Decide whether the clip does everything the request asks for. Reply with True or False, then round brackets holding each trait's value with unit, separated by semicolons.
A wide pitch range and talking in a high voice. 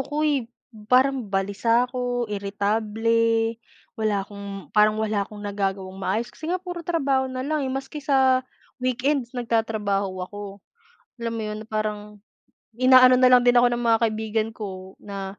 False (3.8 semitones; 225 Hz)